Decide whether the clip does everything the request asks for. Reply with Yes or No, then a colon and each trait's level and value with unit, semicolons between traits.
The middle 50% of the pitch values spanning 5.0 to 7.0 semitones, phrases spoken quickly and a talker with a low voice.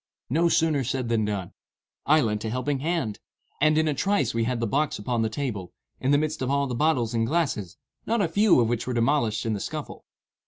Yes: average, 5.3 semitones; fast, 230 wpm; low, 130 Hz